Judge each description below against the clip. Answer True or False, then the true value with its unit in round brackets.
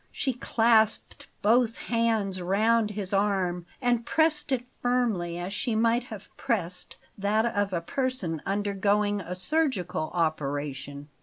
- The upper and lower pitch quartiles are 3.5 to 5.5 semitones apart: True (4.5 semitones)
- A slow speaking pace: True (130 wpm)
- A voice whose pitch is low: False (205 Hz)